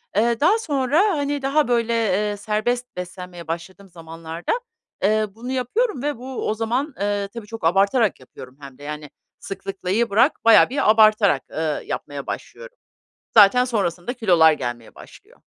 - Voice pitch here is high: Yes, high, 215 Hz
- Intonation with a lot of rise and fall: Yes, wide, 6.1 semitones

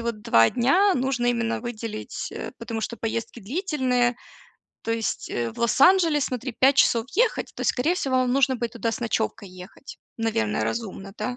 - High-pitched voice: Yes, high, 240 Hz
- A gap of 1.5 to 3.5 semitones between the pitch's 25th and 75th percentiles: Yes, average, 2.9 semitones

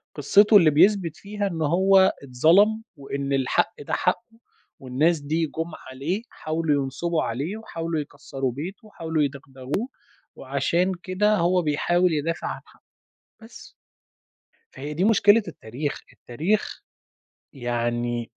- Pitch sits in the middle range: Yes, medium, 160 Hz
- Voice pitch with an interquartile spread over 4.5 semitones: Yes, wide, 5.4 semitones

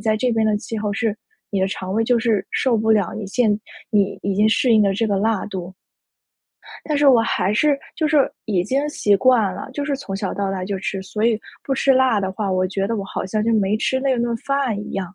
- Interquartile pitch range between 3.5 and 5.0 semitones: Yes, average, 3.9 semitones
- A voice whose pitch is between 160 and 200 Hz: No, high, 215 Hz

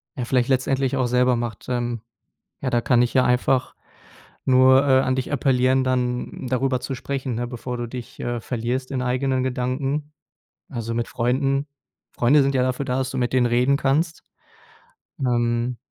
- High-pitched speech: No, low, 130 Hz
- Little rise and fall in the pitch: Yes, narrow, 1.5 semitones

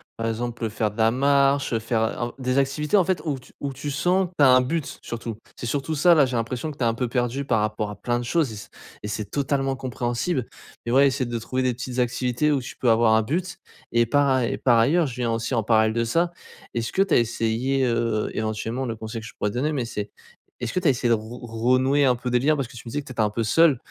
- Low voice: Yes, low, 125 Hz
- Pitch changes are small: No, average, 3.3 semitones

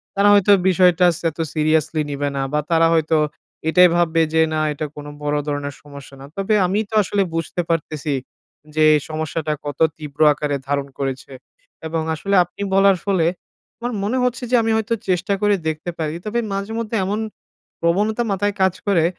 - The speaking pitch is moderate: Yes, medium, 165 Hz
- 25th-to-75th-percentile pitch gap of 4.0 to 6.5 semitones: Yes, average, 4.6 semitones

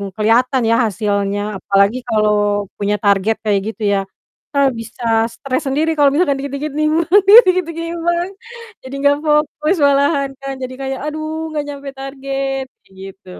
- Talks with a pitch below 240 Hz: No, very high, 275 Hz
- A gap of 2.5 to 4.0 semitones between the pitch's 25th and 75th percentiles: No, wide, 5.5 semitones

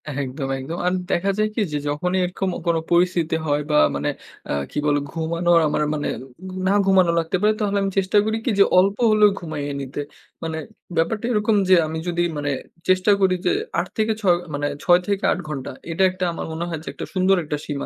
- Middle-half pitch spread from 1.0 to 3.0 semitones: No, average, 4.3 semitones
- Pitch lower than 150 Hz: No, medium, 175 Hz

